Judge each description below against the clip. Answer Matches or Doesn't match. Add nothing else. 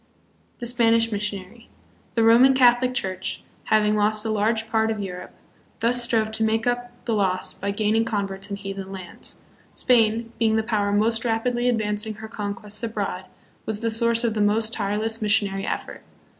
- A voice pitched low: Doesn't match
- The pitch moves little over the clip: Matches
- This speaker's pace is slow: Doesn't match